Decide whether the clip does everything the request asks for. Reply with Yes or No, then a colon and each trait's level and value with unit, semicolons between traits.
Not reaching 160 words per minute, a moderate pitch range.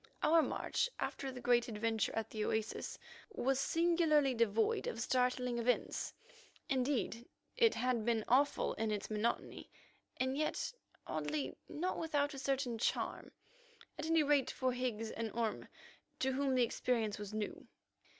Yes: average, 145 wpm; average, 4.2 semitones